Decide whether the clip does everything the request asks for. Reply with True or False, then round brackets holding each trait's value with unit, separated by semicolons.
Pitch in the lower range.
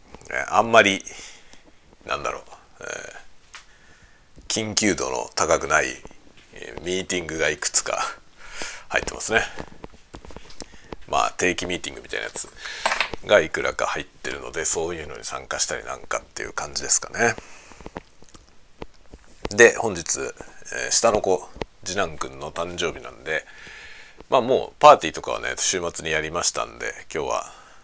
False (275 Hz)